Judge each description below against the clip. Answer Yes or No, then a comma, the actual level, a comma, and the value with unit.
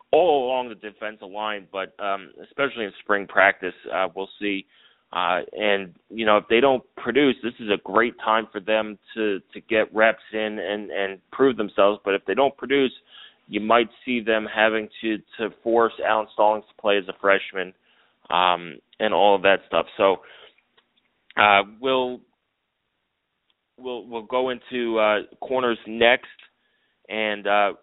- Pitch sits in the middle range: No, low, 110 Hz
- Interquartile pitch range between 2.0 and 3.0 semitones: Yes, narrow, 2.4 semitones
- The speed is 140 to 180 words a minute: Yes, average, 165 wpm